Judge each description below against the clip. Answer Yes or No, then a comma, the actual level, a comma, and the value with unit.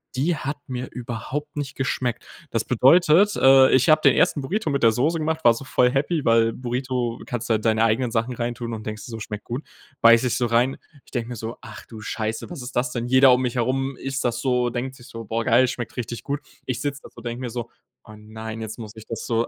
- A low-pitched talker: Yes, low, 125 Hz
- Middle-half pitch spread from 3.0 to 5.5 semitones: No, narrow, 2.6 semitones